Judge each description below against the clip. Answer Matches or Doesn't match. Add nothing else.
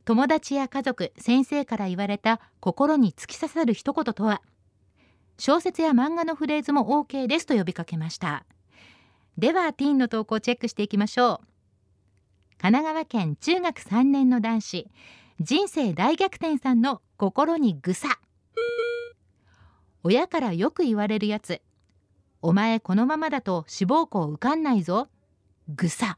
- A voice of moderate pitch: Doesn't match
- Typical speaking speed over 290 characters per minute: Doesn't match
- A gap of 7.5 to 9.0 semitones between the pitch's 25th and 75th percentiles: Matches